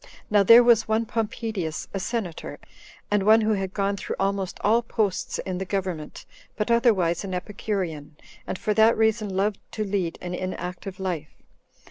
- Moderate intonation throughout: Yes, average, 3.1 semitones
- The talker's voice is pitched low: No, high, 200 Hz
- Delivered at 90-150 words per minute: No, average, 165 wpm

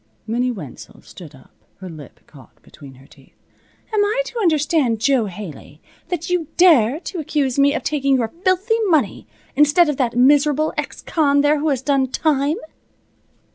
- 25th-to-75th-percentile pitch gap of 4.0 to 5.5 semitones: Yes, average, 5.1 semitones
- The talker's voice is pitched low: No, very high, 280 Hz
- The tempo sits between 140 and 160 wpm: No, average, 170 wpm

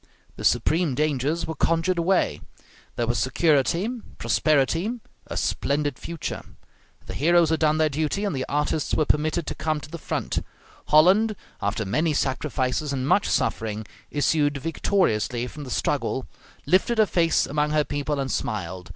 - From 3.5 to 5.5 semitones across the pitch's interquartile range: Yes, average, 3.8 semitones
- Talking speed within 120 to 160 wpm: Yes, average, 155 wpm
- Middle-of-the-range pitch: Yes, medium, 150 Hz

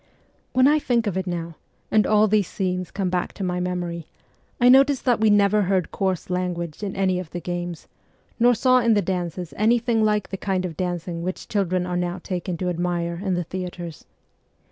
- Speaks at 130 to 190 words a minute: No, average, 200 wpm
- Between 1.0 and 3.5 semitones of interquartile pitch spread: Yes, average, 3.1 semitones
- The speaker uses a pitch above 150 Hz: Yes, medium, 185 Hz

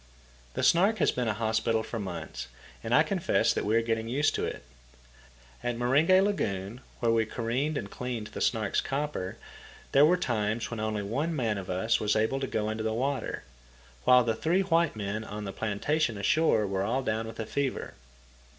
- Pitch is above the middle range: No, low, 115 Hz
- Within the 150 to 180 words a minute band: No, average, 190 wpm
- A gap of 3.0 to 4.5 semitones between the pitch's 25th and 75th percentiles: Yes, average, 4.1 semitones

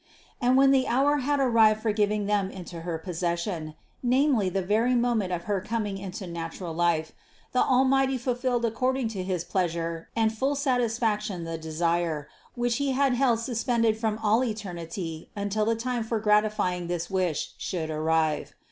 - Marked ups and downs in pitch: Yes, wide, 5.8 semitones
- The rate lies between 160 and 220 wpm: Yes, average, 165 wpm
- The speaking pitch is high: Yes, high, 210 Hz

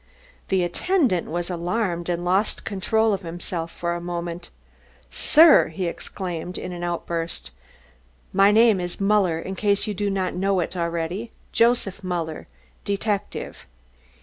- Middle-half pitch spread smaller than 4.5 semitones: Yes, average, 2.8 semitones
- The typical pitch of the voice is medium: Yes, medium, 180 Hz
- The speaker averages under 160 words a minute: Yes, average, 140 wpm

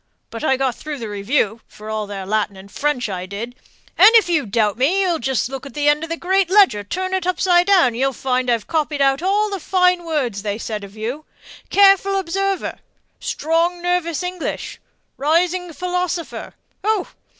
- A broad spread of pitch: Yes, wide, 7.7 semitones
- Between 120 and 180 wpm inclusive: No, average, 190 wpm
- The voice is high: Yes, very high, 305 Hz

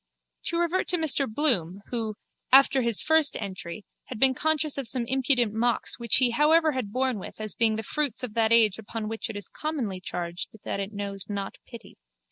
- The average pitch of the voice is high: Yes, high, 235 Hz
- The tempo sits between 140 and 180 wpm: No, average, 200 wpm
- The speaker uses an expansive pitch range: No, average, 4.7 semitones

